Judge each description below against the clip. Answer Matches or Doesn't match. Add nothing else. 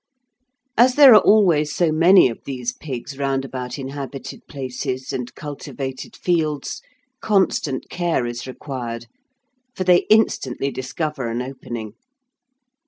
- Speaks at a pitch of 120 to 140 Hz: Matches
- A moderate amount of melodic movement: Matches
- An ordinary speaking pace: Doesn't match